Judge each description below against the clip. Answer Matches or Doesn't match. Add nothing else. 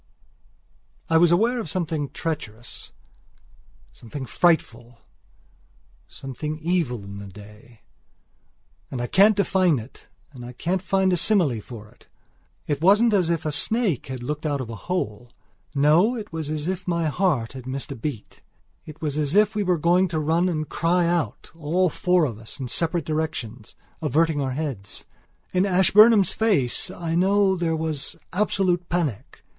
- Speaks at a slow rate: Doesn't match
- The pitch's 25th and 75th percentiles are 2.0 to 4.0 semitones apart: Doesn't match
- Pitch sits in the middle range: Matches